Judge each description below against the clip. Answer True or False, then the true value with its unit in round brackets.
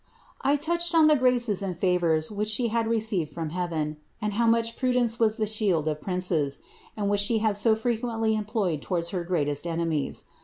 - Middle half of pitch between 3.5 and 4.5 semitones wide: False (5.2 semitones)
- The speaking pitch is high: True (210 Hz)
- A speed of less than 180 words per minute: False (190 wpm)